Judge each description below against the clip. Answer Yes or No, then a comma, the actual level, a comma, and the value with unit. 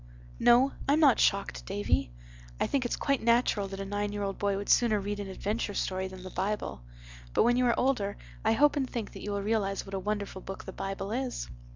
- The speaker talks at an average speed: No, fast, 230 wpm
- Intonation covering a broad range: No, average, 3.4 semitones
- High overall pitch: Yes, high, 205 Hz